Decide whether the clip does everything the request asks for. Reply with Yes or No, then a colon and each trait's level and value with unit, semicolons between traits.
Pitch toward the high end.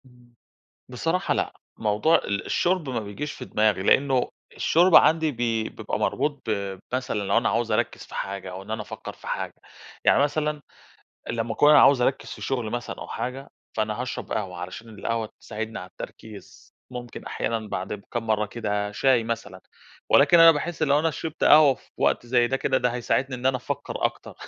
No: low, 120 Hz